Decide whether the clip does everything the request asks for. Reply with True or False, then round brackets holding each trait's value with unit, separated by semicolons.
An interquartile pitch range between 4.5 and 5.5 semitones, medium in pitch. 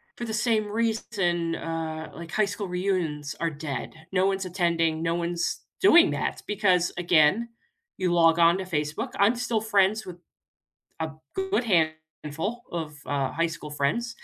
True (4.8 semitones; 175 Hz)